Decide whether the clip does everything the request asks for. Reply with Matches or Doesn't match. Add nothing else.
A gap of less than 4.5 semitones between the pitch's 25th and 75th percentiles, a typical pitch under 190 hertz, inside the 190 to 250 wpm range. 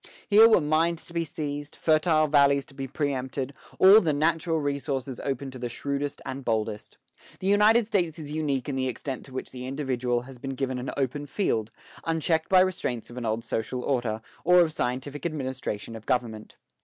Matches